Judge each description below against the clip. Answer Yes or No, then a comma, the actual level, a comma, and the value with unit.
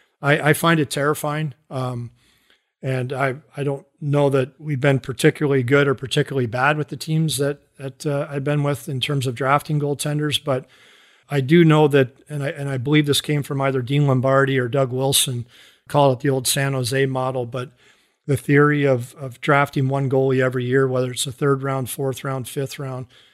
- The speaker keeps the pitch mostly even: Yes, narrow, 1.7 semitones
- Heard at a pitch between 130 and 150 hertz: Yes, medium, 140 Hz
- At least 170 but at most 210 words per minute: Yes, average, 200 wpm